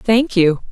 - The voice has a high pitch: Yes, high, 205 Hz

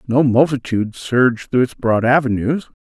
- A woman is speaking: No, male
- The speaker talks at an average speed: Yes, average, 150 wpm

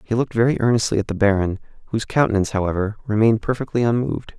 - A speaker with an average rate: Yes, average, 180 wpm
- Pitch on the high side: No, low, 110 Hz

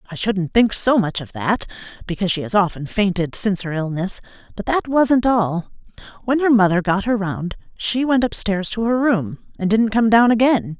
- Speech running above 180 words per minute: Yes, average, 200 wpm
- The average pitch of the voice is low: No, high, 210 Hz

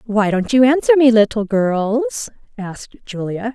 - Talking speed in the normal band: Yes, average, 150 wpm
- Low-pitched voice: No, high, 230 Hz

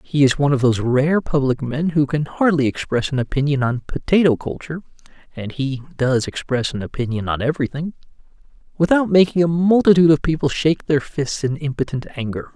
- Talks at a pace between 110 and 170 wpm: Yes, average, 165 wpm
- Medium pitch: Yes, medium, 145 Hz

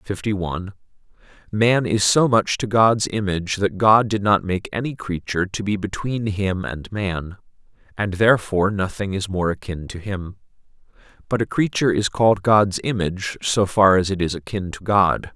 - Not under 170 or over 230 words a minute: Yes, average, 175 wpm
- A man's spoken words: Yes, male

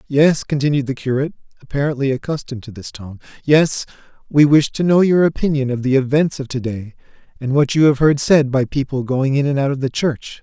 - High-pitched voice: No, medium, 140 Hz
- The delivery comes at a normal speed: No, fast, 215 wpm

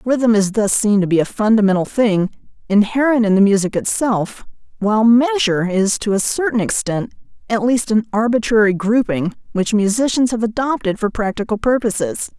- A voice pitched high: Yes, high, 215 Hz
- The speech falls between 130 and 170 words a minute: Yes, average, 160 wpm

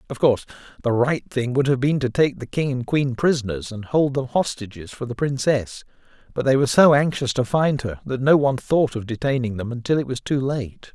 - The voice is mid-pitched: No, low, 130 Hz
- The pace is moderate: No, fast, 230 wpm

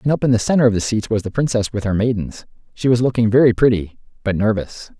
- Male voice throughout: Yes, male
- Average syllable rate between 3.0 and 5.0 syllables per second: No, 6.5 syllables/s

